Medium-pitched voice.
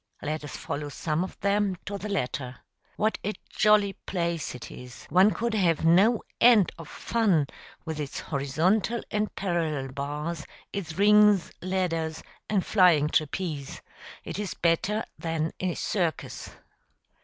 Yes: medium, 175 Hz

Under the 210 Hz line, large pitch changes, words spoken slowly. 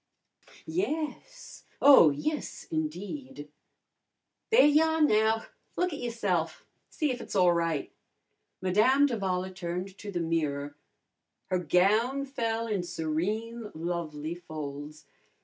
Yes: high, 190 Hz; wide, 7.7 semitones; slow, 105 wpm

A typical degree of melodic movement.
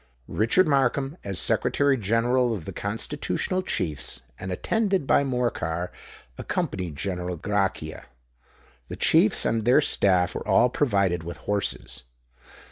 No: wide, 6.8 semitones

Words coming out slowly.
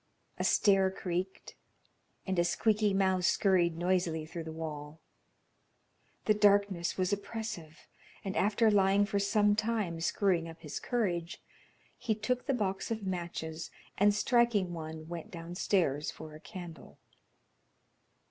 Yes: slow, 130 wpm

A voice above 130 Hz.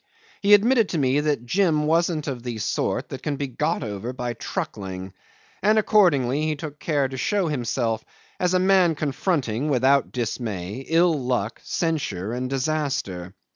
Yes: medium, 140 Hz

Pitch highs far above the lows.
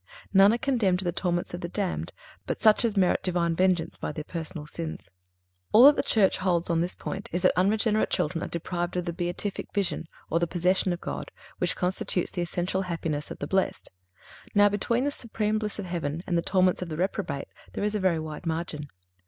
No: average, 2.9 semitones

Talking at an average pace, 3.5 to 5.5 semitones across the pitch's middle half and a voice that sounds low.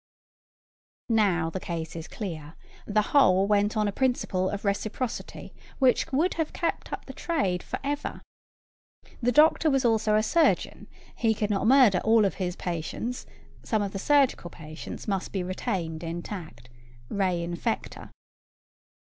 No: average, 145 wpm; average, 5.2 semitones; high, 205 Hz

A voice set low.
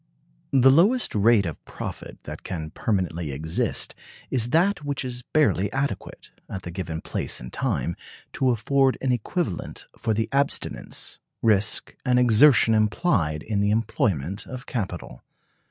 Yes: low, 110 Hz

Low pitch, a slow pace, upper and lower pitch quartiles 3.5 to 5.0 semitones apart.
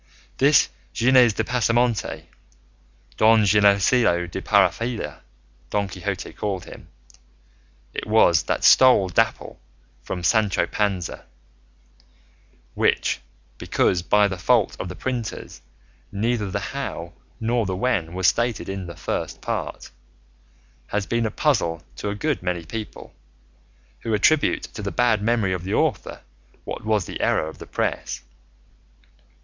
Yes: low, 105 Hz; slow, 130 wpm; average, 4.1 semitones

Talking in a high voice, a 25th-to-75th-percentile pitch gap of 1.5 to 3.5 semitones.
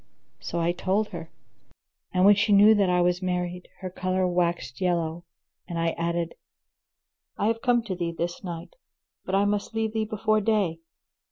No: medium, 180 Hz; average, 3.2 semitones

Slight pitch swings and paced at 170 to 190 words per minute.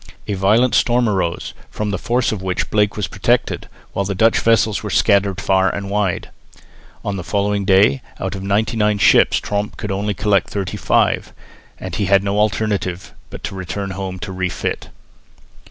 Yes: narrow, 1.6 semitones; average, 175 wpm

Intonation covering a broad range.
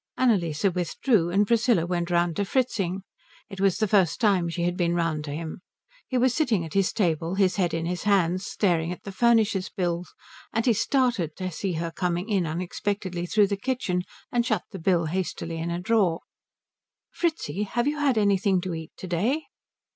No: average, 3.7 semitones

